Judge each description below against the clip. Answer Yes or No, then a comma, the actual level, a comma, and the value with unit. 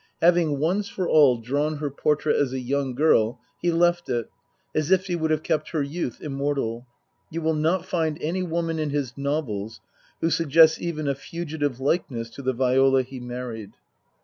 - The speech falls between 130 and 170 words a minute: No, average, 180 wpm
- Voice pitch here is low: No, medium, 150 Hz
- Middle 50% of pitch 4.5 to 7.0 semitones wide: No, average, 3.9 semitones